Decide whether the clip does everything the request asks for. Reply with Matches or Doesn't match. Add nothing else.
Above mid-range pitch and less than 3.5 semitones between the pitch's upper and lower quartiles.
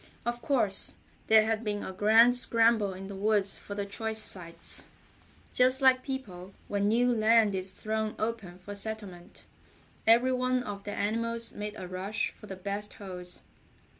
Matches